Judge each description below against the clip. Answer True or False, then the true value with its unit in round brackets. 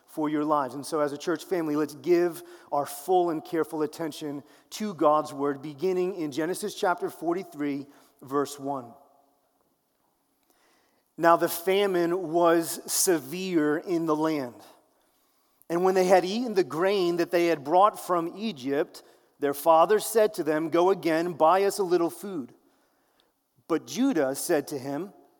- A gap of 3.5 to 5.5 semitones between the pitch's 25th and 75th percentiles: True (3.8 semitones)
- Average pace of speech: True (150 wpm)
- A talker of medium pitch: True (170 Hz)